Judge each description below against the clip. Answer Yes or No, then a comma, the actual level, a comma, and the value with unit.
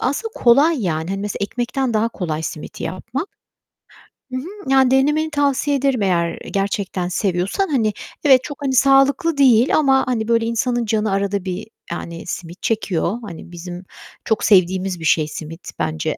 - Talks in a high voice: Yes, high, 220 Hz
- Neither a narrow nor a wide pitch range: No, wide, 6.8 semitones